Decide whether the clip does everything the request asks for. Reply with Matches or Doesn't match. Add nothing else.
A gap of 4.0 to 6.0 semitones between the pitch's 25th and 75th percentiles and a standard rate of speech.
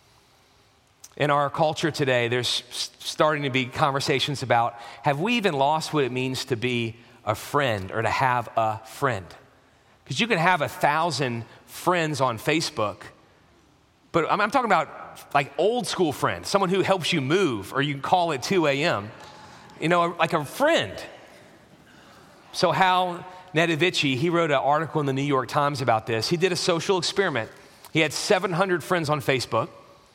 Matches